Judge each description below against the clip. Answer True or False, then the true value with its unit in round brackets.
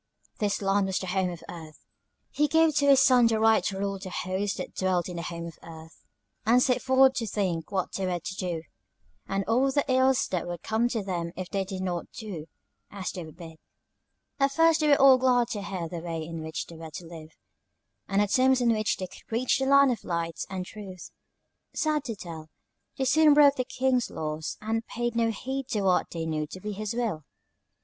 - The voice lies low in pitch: False (200 Hz)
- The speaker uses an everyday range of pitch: False (6.4 semitones)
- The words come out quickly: True (225 wpm)